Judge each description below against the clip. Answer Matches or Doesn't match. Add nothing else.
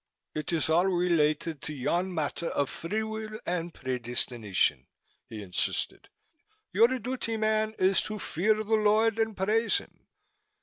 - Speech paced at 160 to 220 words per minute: Doesn't match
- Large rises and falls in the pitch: Matches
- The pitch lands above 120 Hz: Matches